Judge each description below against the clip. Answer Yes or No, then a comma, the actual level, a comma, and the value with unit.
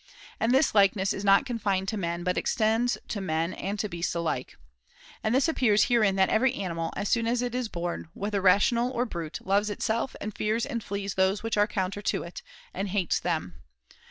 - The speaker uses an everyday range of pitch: Yes, average, 3.6 semitones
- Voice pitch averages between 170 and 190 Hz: No, high, 205 Hz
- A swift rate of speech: Yes, fast, 215 wpm